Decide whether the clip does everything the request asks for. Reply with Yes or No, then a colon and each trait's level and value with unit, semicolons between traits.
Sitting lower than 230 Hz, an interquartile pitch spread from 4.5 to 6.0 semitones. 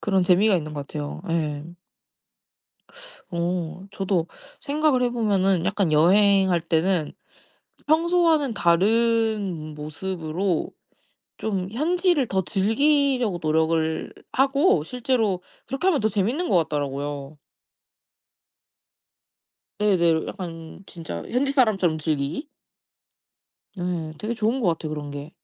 No: high, 190 Hz; wide, 6.4 semitones